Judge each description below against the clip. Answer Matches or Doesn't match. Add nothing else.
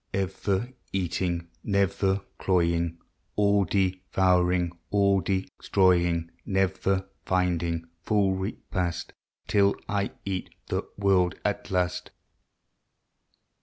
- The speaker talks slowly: Matches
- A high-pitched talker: Doesn't match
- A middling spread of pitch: Doesn't match